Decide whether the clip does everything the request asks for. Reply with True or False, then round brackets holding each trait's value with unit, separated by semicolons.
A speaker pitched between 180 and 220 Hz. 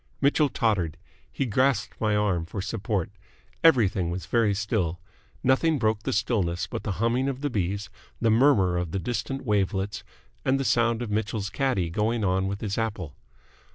False (105 Hz)